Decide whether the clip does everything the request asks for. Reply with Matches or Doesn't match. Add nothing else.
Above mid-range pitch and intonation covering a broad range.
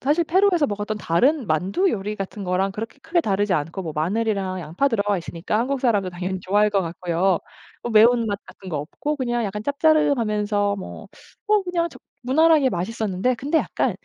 Matches